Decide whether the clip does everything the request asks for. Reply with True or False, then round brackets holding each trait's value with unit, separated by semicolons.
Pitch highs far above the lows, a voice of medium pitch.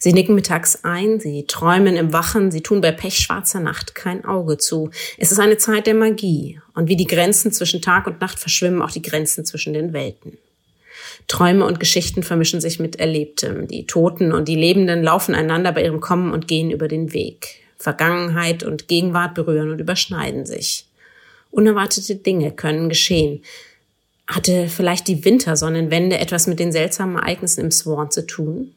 False (2.8 semitones; 175 Hz)